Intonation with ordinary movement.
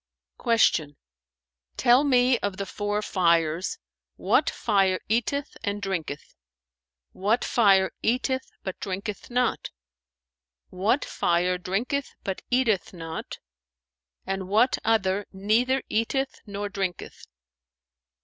Yes: average, 4.2 semitones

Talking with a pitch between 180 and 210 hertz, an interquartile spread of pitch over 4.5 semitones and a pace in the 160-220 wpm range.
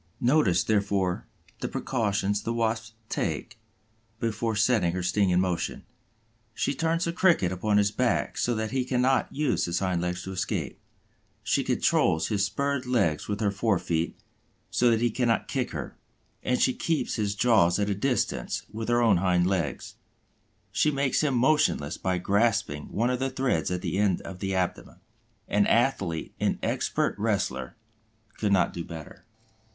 No: low, 105 Hz; average, 5.1 semitones; average, 165 wpm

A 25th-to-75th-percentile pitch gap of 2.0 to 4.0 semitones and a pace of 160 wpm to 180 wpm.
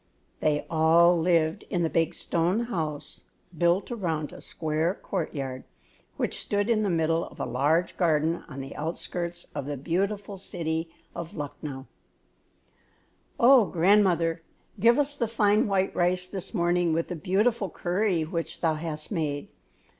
No: average, 3.5 semitones; average, 145 wpm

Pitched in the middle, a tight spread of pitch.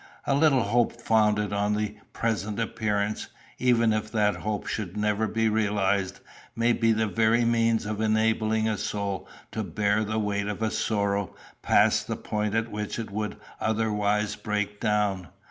No: low, 105 Hz; narrow, 1.3 semitones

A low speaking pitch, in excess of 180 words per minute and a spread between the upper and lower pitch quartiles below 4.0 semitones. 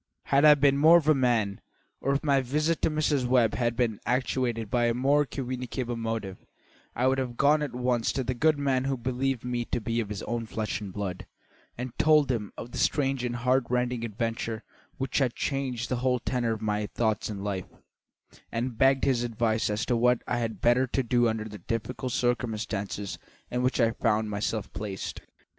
Yes: low, 120 Hz; average, 200 wpm; average, 2.8 semitones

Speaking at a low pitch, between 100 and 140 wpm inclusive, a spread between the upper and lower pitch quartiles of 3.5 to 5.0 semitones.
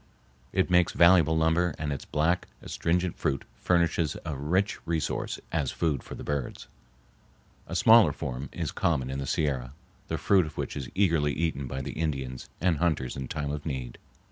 No: very low, 75 Hz; average, 175 wpm; average, 3.9 semitones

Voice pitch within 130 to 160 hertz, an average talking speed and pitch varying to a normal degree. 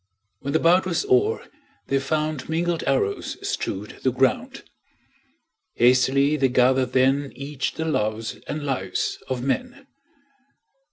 No: medium, 140 Hz; slow, 125 wpm; average, 3.7 semitones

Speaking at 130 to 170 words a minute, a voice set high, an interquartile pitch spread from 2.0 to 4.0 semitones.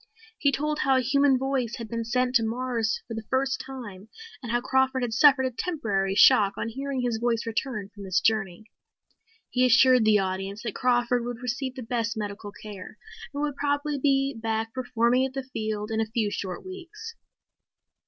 No: average, 190 wpm; high, 240 Hz; average, 3.3 semitones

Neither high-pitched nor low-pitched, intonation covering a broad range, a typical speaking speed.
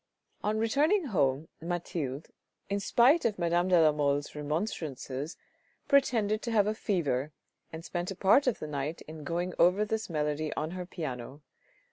Yes: medium, 175 Hz; wide, 5.9 semitones; average, 160 wpm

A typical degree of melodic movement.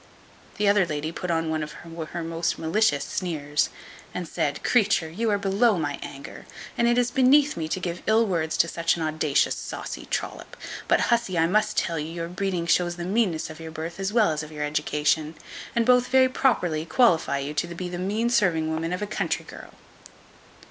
Yes: average, 4.7 semitones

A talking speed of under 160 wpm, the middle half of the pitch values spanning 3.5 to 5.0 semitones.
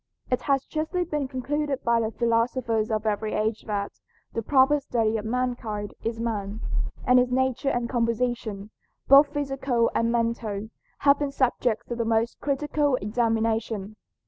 No: average, 150 wpm; average, 3.1 semitones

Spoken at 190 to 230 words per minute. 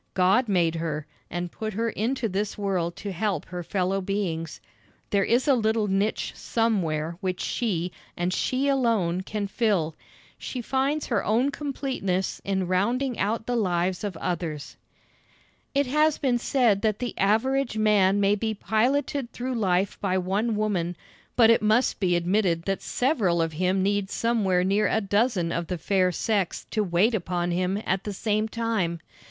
No: average, 165 wpm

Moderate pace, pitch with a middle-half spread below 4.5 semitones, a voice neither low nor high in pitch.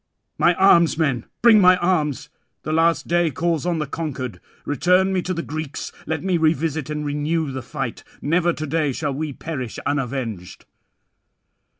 Yes: average, 170 wpm; average, 3.1 semitones; medium, 155 Hz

